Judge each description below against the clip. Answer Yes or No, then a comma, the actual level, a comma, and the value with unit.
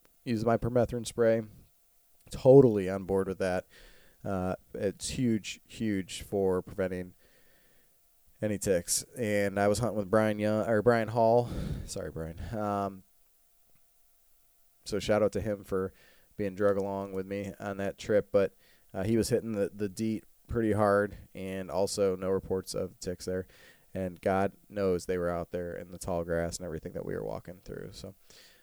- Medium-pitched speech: No, low, 100 Hz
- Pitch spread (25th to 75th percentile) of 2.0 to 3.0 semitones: Yes, narrow, 2.6 semitones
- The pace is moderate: Yes, average, 170 wpm